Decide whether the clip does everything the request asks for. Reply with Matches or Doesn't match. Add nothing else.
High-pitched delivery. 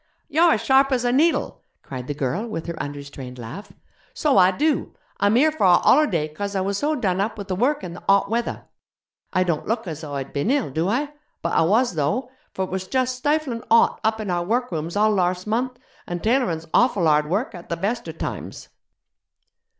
Matches